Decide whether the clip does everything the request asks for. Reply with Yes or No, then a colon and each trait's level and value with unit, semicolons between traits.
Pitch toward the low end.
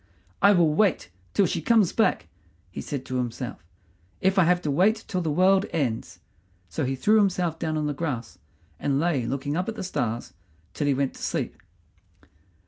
No: medium, 160 Hz